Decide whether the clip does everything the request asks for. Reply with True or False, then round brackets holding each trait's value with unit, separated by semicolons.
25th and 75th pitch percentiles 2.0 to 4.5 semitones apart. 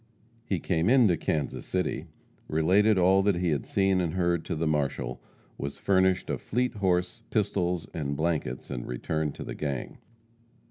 True (3.7 semitones)